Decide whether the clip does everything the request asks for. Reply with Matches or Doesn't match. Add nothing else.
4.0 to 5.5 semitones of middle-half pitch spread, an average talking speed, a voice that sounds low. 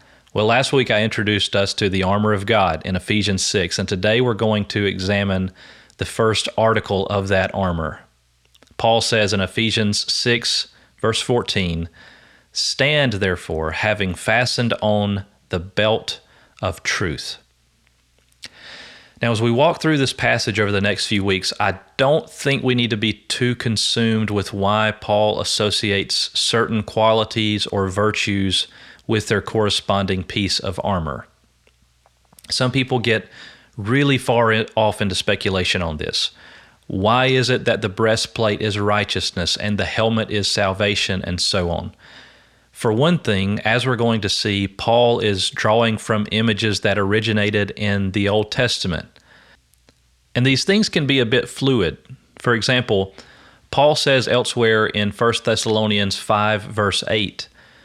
Doesn't match